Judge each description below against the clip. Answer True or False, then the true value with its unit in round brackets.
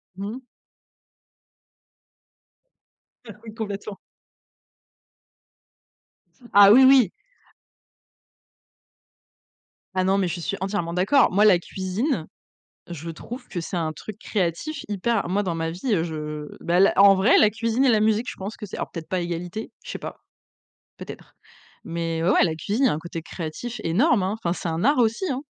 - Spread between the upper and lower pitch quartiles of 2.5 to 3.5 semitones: False (4.6 semitones)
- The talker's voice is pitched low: False (195 Hz)